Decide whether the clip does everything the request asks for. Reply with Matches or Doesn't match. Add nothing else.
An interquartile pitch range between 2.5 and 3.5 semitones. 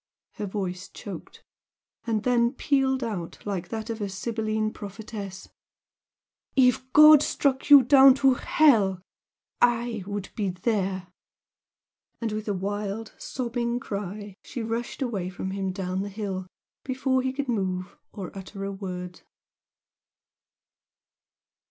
Doesn't match